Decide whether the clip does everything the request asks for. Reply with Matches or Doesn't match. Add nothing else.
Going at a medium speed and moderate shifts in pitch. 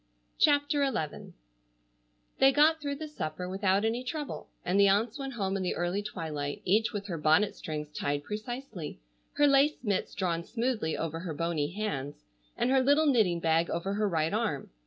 Doesn't match